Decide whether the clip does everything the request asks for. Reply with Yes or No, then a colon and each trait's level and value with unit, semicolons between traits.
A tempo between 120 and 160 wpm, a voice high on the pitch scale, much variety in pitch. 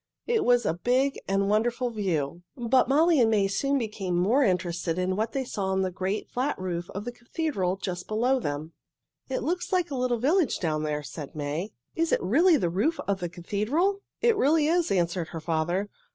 No: average, 200 wpm; high, 210 Hz; wide, 7.2 semitones